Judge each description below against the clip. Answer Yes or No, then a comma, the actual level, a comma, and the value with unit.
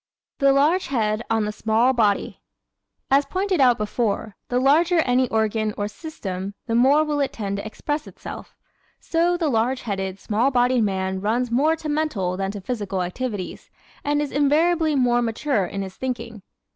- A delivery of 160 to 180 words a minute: Yes, average, 175 wpm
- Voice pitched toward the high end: Yes, high, 240 Hz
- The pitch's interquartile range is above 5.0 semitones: Yes, wide, 5.5 semitones